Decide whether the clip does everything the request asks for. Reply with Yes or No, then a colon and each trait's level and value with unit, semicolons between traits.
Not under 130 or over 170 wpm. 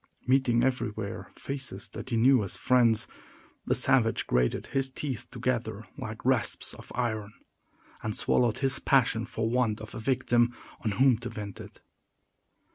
Yes: average, 150 wpm